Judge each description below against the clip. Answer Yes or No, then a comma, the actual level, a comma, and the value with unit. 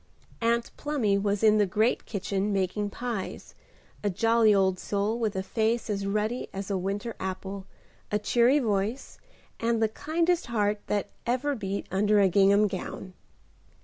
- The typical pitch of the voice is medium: No, high, 210 Hz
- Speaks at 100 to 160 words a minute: Yes, average, 155 wpm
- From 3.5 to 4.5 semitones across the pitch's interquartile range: No, average, 2.8 semitones